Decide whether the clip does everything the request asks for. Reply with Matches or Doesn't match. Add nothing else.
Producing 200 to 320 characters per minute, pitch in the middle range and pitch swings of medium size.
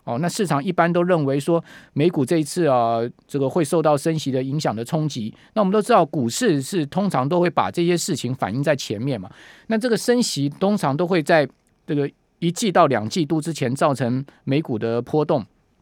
Matches